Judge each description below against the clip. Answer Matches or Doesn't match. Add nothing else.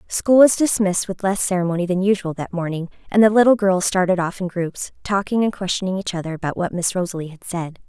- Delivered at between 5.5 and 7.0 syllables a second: Matches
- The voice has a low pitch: Doesn't match